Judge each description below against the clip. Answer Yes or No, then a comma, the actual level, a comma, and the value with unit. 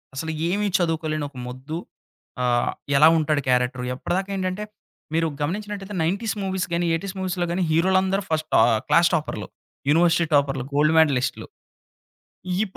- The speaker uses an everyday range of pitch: Yes, average, 4.4 semitones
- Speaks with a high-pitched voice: No, medium, 165 Hz